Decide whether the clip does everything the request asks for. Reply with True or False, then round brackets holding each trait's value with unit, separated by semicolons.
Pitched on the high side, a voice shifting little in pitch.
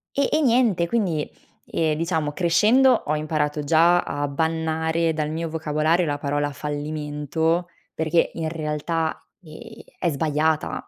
False (160 Hz; 2.0 semitones)